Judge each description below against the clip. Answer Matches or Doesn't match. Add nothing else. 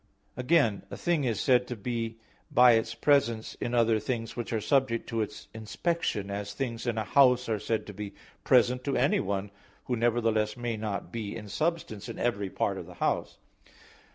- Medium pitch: Doesn't match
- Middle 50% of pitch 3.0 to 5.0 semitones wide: Doesn't match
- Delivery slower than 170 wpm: Doesn't match